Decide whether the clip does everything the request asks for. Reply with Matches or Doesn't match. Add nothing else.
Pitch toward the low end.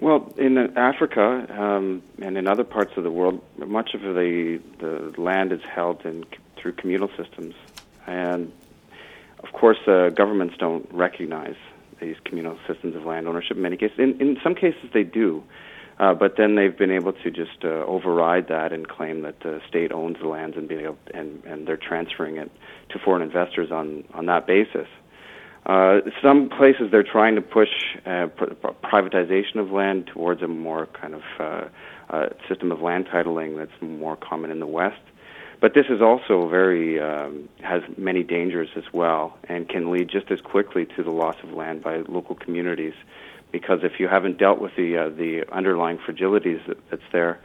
Matches